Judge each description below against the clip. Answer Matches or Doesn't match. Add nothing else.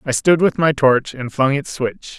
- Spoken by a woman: Doesn't match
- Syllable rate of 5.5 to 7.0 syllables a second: Doesn't match